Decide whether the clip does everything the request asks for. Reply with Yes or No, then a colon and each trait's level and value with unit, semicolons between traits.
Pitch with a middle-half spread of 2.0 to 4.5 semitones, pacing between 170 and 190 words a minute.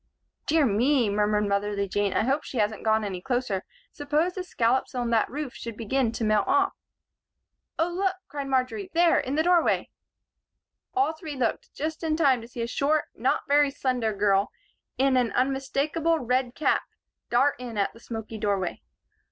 No: wide, 5.4 semitones; average, 175 wpm